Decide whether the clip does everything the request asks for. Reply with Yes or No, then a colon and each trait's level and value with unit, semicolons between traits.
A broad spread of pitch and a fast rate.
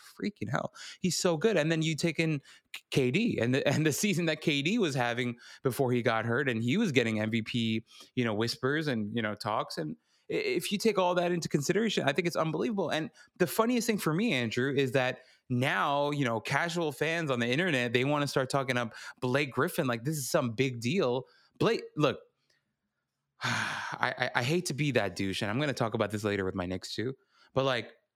Yes: wide, 5.9 semitones; fast, 220 wpm